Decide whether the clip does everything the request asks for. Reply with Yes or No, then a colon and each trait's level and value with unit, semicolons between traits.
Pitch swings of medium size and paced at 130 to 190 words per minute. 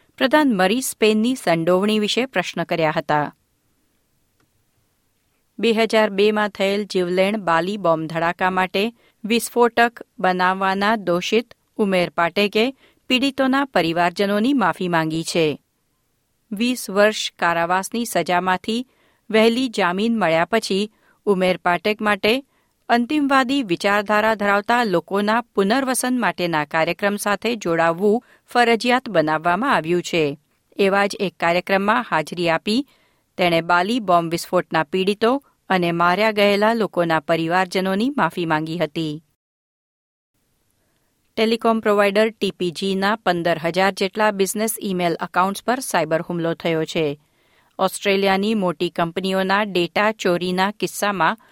No: average, 4.2 semitones; average, 105 wpm